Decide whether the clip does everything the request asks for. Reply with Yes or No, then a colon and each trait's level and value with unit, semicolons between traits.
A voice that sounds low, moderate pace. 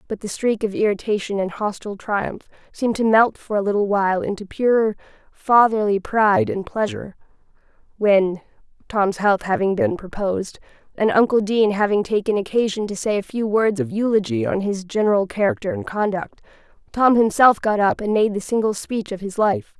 No: high, 210 Hz; average, 175 wpm